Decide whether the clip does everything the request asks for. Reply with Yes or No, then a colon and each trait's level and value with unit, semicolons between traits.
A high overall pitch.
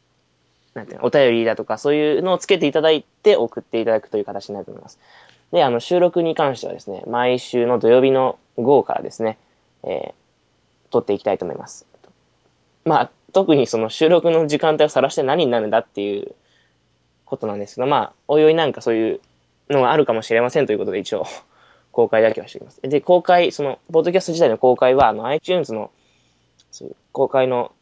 No: low, 120 Hz